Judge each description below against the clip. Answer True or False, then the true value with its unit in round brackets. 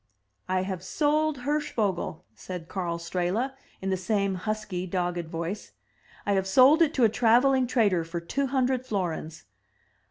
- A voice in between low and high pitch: False (200 Hz)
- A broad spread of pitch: True (6.1 semitones)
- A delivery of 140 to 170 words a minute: True (155 wpm)